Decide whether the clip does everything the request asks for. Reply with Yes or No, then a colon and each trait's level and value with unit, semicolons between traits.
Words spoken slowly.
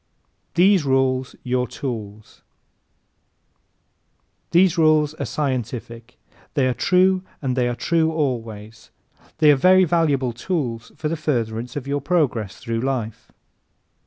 Yes: slow, 130 wpm